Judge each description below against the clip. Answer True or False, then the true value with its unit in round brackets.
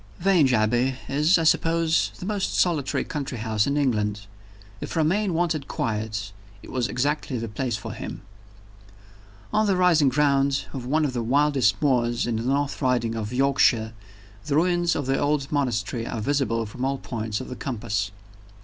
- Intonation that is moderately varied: True (4.6 semitones)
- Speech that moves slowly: False (175 wpm)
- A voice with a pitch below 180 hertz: True (135 Hz)